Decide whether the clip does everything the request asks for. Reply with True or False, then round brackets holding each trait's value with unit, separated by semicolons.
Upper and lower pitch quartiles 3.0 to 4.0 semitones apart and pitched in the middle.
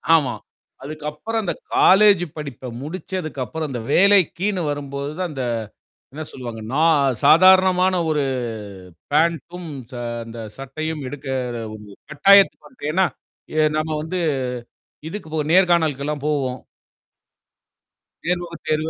False (4.4 semitones; 155 Hz)